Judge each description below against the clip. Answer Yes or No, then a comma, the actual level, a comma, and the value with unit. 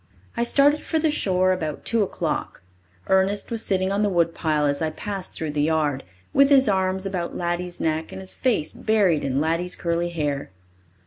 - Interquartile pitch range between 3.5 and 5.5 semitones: Yes, average, 4.3 semitones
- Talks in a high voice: No, medium, 180 Hz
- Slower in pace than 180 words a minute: No, average, 185 wpm